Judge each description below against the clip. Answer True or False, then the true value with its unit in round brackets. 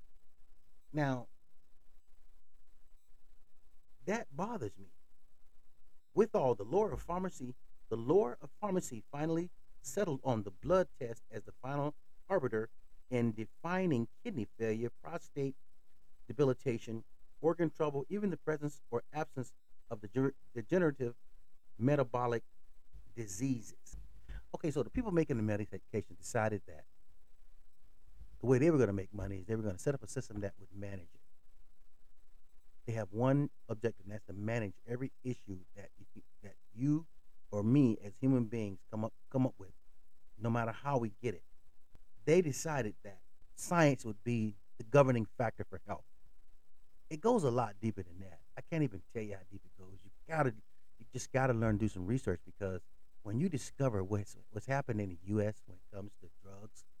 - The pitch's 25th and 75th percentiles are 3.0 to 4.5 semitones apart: False (5.3 semitones)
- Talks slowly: False (160 wpm)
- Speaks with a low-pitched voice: True (110 Hz)